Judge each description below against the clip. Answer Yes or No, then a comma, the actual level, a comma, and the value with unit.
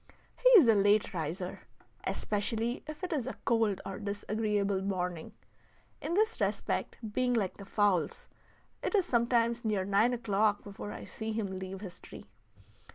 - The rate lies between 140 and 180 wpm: Yes, average, 160 wpm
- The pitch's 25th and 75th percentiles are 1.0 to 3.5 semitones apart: Yes, average, 3.2 semitones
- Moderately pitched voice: No, high, 210 Hz